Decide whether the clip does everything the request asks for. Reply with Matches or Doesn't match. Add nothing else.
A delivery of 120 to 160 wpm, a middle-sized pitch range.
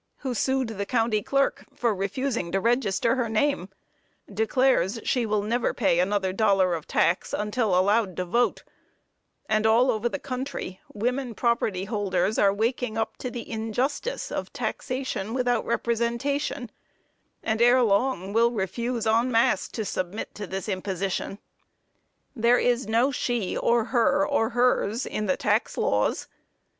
Matches